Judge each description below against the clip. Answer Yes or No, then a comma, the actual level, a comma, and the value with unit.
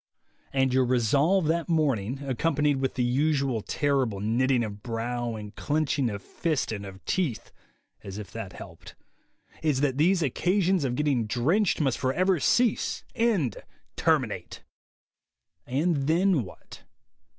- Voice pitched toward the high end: No, low, 135 Hz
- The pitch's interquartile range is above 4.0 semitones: Yes, average, 5.1 semitones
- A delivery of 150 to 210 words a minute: No, slow, 135 wpm